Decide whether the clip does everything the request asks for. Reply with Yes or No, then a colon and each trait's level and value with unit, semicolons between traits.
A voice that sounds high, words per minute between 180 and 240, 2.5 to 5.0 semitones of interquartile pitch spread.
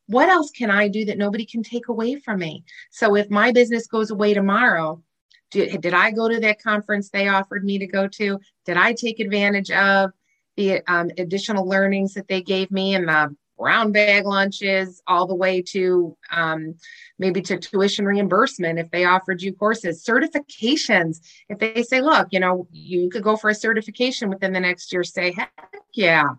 Yes: high, 200 Hz; average, 190 wpm; average, 3.2 semitones